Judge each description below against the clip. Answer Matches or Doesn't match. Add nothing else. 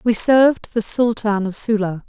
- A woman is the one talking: Matches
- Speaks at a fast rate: Doesn't match